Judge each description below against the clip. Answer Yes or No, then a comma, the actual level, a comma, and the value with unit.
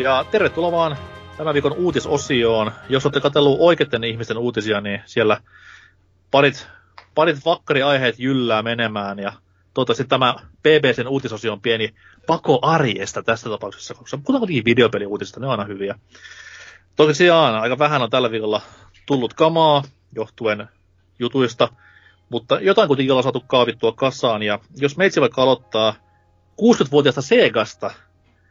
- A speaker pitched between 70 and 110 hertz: No, low, 125 Hz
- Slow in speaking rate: No, average, 135 wpm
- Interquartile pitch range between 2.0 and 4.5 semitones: No, wide, 5.5 semitones